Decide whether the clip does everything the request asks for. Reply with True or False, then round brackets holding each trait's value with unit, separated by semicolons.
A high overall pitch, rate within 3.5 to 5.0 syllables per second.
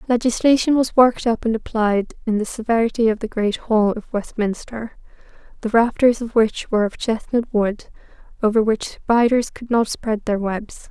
True (225 Hz; 4.9 syllables/s)